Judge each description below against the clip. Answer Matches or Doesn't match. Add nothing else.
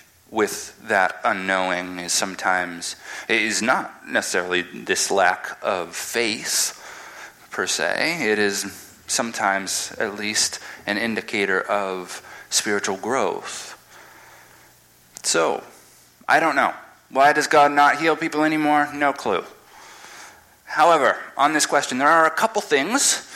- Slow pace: Matches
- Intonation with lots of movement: Matches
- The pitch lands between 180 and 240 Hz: Doesn't match